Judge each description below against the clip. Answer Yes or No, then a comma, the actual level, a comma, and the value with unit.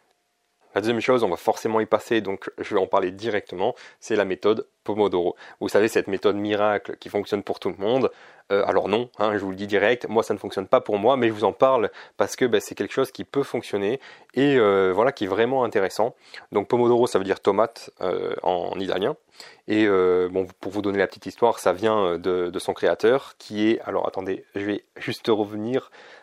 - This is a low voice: Yes, low, 105 Hz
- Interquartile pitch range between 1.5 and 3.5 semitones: Yes, average, 3.0 semitones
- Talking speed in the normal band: No, fast, 225 wpm